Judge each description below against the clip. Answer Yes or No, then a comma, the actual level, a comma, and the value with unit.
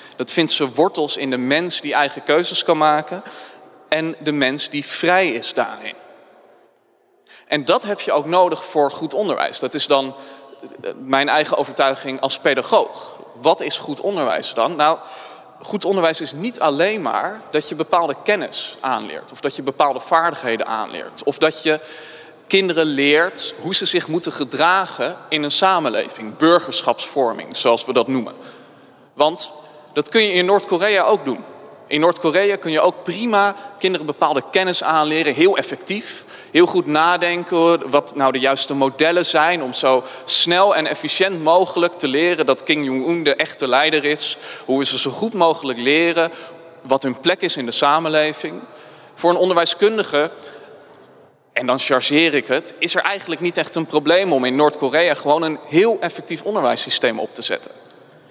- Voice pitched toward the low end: No, medium, 160 Hz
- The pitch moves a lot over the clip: No, average, 3.6 semitones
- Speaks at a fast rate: No, average, 165 wpm